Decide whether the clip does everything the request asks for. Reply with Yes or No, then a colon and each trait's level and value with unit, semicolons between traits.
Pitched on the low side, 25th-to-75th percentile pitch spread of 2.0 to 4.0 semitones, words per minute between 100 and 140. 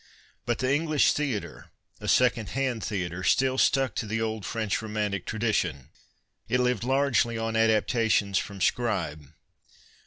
Yes: low, 115 Hz; average, 3.7 semitones; slow, 135 wpm